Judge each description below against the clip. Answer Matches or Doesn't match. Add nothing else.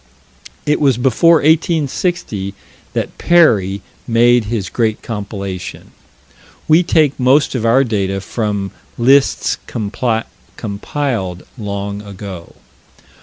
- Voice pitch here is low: Matches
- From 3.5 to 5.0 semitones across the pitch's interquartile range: Doesn't match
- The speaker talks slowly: Matches